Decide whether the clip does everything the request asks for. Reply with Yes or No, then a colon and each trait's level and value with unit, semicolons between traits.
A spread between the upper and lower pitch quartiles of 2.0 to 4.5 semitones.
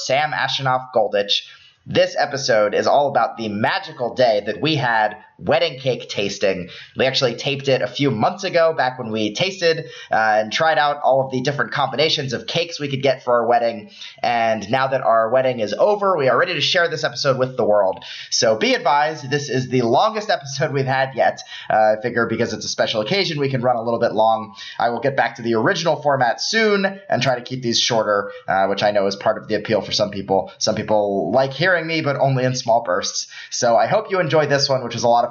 No: average, 5.0 semitones